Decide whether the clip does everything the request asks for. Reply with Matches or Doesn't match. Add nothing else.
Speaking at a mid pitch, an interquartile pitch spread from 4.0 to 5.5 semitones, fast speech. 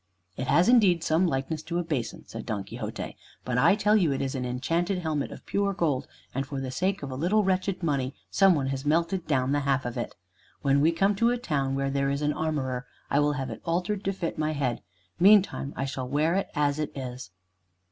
Matches